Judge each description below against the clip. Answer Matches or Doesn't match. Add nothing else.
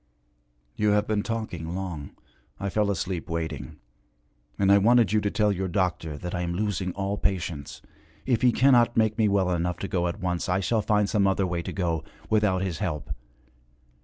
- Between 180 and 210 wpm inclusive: Matches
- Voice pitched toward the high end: Doesn't match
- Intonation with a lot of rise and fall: Doesn't match